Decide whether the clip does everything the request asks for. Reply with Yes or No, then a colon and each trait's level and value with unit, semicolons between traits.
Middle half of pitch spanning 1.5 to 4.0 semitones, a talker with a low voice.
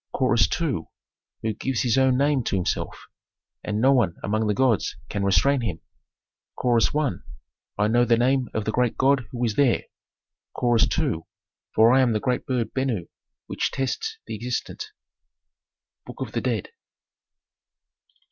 Yes: average, 3.4 semitones; low, 120 Hz